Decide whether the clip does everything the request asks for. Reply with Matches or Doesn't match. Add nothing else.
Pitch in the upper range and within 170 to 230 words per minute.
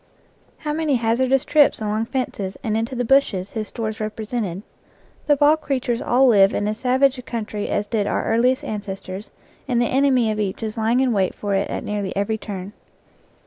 Matches